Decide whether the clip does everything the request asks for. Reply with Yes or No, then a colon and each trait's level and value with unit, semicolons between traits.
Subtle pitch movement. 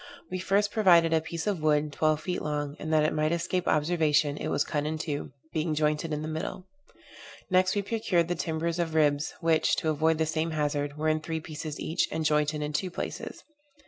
Yes: narrow, 1.9 semitones